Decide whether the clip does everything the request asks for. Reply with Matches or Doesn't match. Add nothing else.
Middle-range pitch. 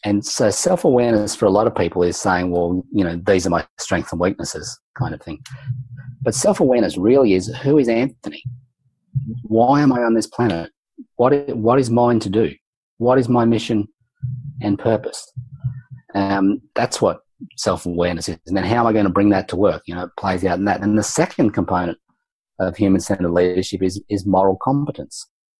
Doesn't match